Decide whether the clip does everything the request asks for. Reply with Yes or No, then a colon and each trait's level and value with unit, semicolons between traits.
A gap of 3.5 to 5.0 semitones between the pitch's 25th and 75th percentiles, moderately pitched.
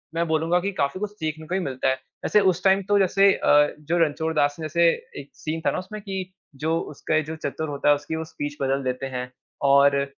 Yes: average, 4.0 semitones; medium, 160 Hz